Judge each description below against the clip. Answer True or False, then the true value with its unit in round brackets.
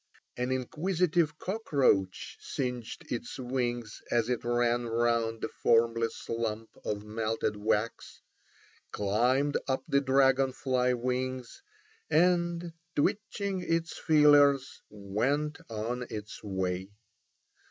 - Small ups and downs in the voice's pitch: False (4.2 semitones)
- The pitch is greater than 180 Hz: False (125 Hz)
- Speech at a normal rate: False (100 wpm)